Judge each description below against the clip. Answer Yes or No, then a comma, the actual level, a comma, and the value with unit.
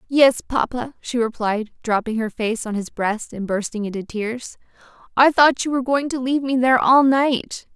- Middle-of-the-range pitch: No, high, 240 Hz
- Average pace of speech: Yes, average, 195 wpm